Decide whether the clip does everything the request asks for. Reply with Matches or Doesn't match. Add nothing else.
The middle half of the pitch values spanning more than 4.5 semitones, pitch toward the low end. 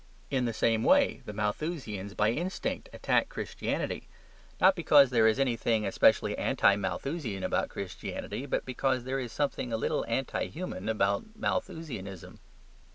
Matches